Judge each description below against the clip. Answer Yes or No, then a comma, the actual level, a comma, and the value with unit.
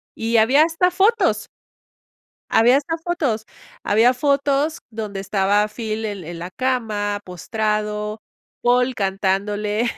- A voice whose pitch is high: Yes, high, 220 Hz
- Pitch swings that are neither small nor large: Yes, average, 4.4 semitones